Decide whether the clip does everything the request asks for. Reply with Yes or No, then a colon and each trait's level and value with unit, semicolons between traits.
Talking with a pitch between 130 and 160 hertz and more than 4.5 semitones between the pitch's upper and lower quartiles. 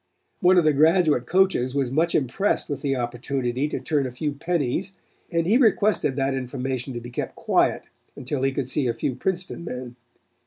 Yes: medium, 140 Hz; average, 5.0 semitones